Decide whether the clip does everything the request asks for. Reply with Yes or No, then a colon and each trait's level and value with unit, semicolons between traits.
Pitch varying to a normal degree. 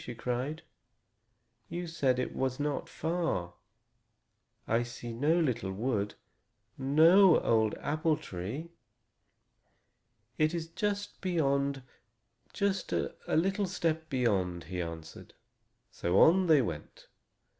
No: wide, 6.5 semitones